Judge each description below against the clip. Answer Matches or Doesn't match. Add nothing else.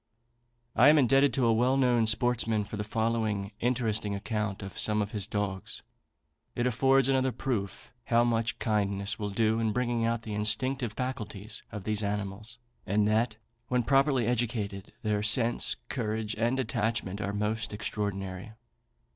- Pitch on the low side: Matches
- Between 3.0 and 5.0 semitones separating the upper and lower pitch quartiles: Doesn't match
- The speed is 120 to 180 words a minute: Matches